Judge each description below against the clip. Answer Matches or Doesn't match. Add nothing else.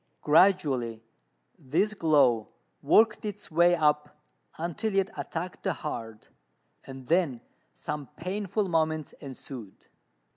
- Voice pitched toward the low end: Doesn't match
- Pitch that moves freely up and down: Matches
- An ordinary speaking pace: Doesn't match